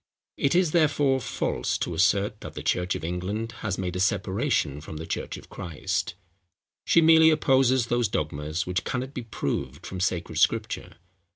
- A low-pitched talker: Yes, low, 105 Hz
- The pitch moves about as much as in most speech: No, wide, 6.9 semitones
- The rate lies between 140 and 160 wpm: No, average, 170 wpm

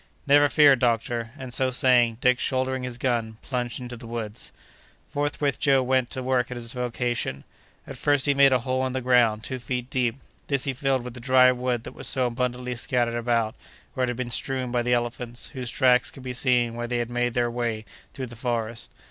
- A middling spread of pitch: No, narrow, 1.5 semitones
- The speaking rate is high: Yes, fast, 215 wpm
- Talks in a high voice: No, low, 125 Hz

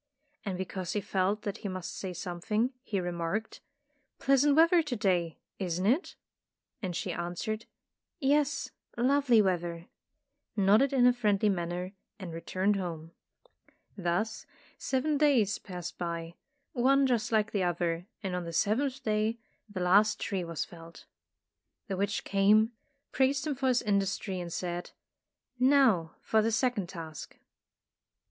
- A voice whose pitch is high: Yes, high, 200 Hz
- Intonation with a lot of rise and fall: Yes, wide, 5.7 semitones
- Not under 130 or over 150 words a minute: Yes, average, 140 wpm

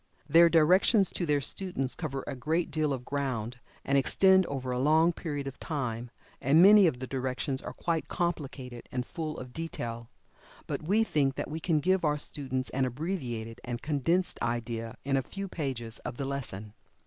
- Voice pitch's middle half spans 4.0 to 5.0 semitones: Yes, average, 4.6 semitones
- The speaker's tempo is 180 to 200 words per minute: Yes, average, 185 wpm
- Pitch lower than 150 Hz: Yes, medium, 140 Hz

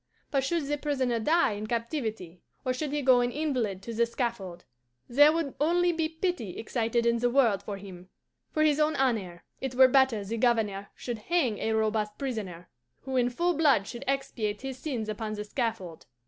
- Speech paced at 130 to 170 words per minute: No, average, 190 wpm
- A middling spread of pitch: Yes, average, 4.6 semitones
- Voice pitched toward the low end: No, high, 240 Hz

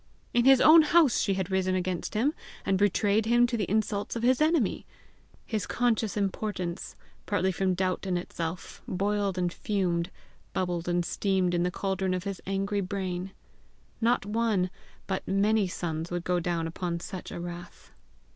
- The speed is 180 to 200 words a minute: No, average, 165 wpm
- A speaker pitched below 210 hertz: Yes, high, 190 Hz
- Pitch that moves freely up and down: No, average, 3.1 semitones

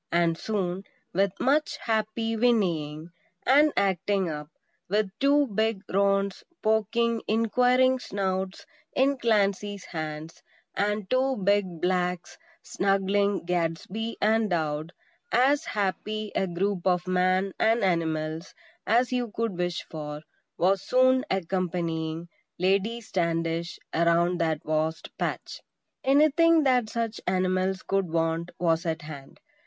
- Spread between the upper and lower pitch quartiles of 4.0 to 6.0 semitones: Yes, average, 4.7 semitones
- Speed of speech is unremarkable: No, slow, 115 wpm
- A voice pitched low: No, high, 195 Hz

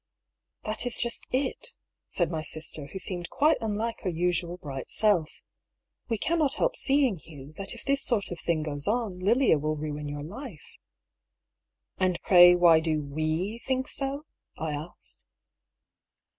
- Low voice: No, medium, 180 Hz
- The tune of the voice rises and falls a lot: Yes, wide, 7.0 semitones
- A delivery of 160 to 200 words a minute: Yes, average, 170 wpm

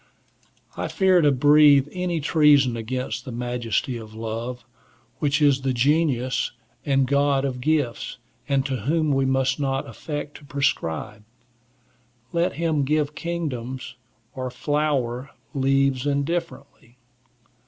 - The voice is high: No, low, 135 Hz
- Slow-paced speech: Yes, slow, 120 wpm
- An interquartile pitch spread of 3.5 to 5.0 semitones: No, average, 2.9 semitones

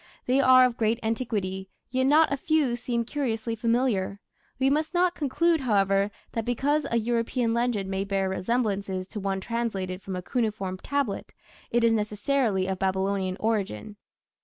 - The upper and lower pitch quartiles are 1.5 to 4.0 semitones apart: No, average, 4.5 semitones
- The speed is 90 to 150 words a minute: No, average, 160 wpm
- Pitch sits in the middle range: No, high, 225 Hz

